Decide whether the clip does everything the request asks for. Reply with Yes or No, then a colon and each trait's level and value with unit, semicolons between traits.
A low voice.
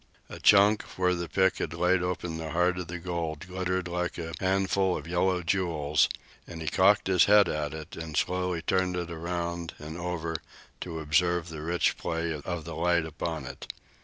Yes: very low, 85 Hz